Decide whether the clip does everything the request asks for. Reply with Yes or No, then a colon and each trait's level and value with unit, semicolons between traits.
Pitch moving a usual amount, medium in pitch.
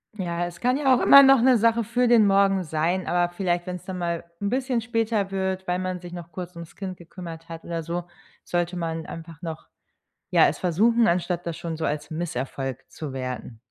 Yes: average, 3.3 semitones; medium, 175 Hz